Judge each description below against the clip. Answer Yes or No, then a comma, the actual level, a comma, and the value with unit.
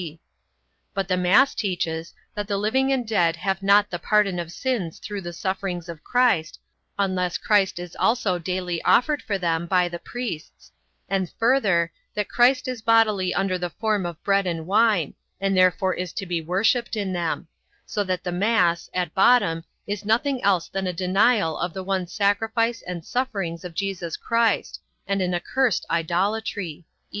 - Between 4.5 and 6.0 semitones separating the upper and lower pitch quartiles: No, average, 3.6 semitones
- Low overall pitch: No, high, 190 Hz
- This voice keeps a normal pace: Yes, average, 170 wpm